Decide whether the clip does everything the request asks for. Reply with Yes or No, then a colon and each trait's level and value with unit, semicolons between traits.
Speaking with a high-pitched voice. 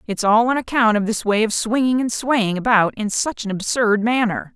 Yes: high, 225 Hz